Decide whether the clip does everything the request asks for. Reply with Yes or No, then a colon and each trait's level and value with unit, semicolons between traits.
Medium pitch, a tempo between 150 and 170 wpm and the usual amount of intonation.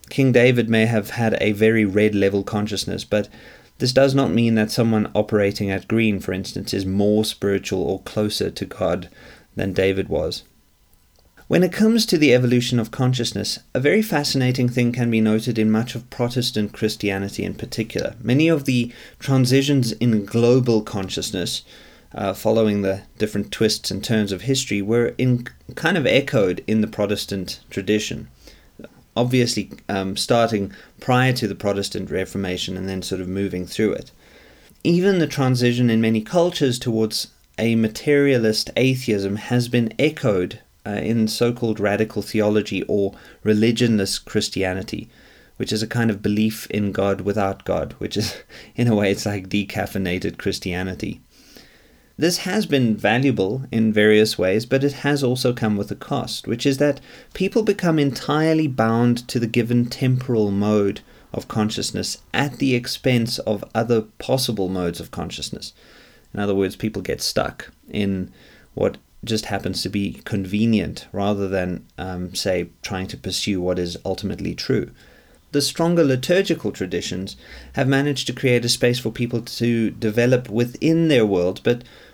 No: low, 110 Hz; average, 155 wpm; average, 3.7 semitones